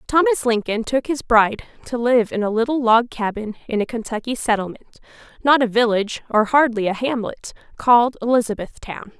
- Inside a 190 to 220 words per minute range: No, average, 150 wpm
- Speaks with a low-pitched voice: No, high, 230 Hz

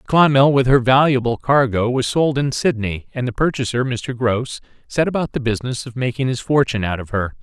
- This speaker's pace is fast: Yes, fast, 210 wpm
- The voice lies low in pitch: Yes, low, 125 Hz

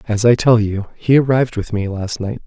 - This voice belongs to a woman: No, male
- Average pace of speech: No, fast, 245 wpm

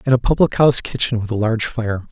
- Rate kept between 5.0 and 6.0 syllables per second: No, 6.6 syllables/s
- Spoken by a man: Yes, male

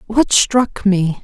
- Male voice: No, female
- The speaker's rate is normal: Yes, average, 145 wpm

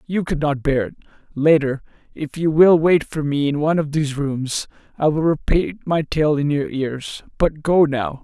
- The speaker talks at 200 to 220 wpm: Yes, fast, 205 wpm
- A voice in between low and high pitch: Yes, medium, 150 Hz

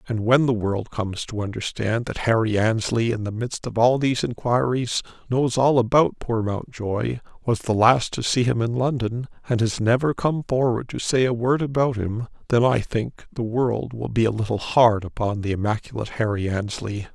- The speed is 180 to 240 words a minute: Yes, average, 190 wpm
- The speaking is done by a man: Yes, male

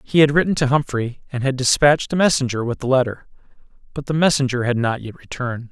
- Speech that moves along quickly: Yes, fast, 210 wpm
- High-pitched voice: No, low, 135 Hz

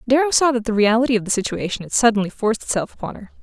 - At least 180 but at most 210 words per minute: No, fast, 245 wpm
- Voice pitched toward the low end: No, high, 230 Hz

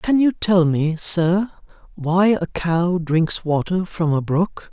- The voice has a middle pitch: Yes, medium, 175 Hz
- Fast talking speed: No, average, 165 wpm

